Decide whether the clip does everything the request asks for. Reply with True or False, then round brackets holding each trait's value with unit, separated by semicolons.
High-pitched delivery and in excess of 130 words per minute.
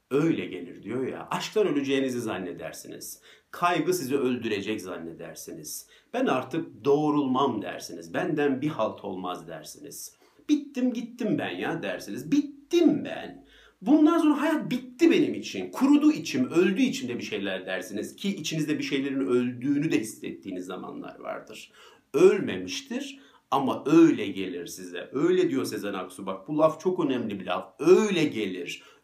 False (175 Hz; 140 wpm)